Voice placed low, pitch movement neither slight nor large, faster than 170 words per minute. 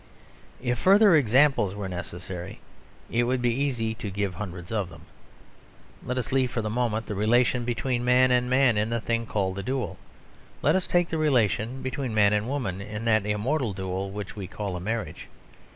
Yes: low, 115 Hz; average, 3.9 semitones; average, 190 wpm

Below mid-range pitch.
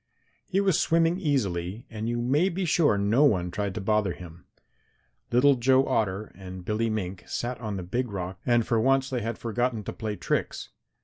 Yes: low, 115 Hz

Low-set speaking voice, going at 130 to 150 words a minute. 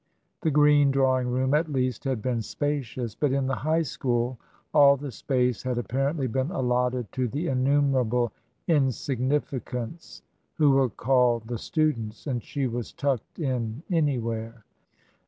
Yes: low, 130 Hz; average, 145 wpm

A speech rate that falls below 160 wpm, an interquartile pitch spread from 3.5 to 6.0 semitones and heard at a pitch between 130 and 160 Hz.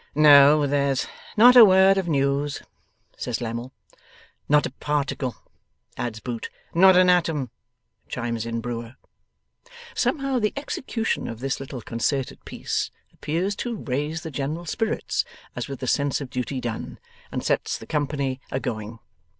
Yes: average, 145 wpm; average, 5.2 semitones; medium, 140 Hz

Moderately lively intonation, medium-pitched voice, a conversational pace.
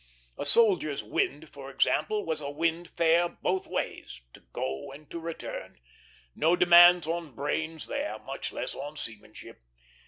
Yes: average, 3.1 semitones; medium, 165 Hz; average, 150 wpm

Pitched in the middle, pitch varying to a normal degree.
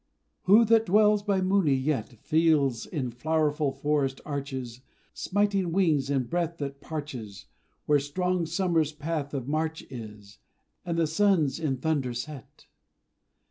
Yes: medium, 150 Hz; average, 4.2 semitones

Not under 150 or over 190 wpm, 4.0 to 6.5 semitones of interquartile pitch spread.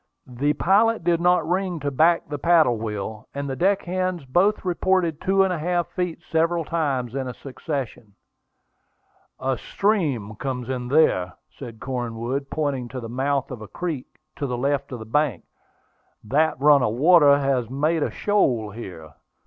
Yes: average, 160 wpm; wide, 5.5 semitones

